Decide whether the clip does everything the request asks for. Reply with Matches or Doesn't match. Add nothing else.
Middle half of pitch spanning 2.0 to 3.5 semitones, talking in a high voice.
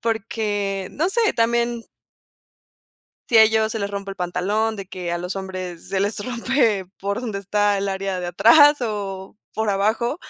Matches